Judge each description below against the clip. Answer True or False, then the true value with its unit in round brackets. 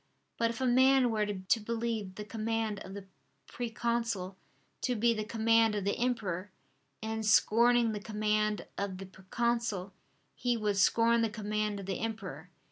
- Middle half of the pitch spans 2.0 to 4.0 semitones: True (2.4 semitones)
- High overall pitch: True (220 Hz)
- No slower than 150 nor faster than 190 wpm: True (160 wpm)